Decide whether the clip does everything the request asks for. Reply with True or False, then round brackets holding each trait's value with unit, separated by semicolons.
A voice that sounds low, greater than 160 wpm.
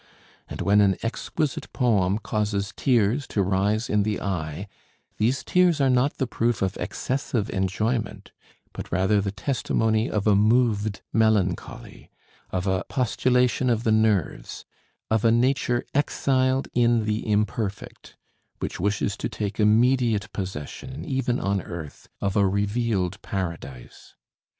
False (105 Hz; 135 wpm)